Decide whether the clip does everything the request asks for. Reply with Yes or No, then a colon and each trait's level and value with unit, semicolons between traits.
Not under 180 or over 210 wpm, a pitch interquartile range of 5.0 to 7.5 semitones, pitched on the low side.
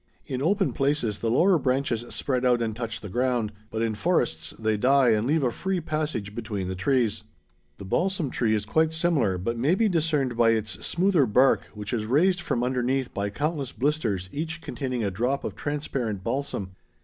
Yes: average, 190 wpm; wide, 5.5 semitones; low, 125 Hz